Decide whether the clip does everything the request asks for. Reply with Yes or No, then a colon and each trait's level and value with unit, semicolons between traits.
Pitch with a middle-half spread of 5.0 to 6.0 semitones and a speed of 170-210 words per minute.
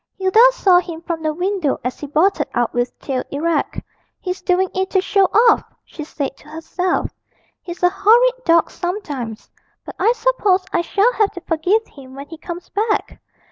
No: average, 4.4 semitones; average, 180 wpm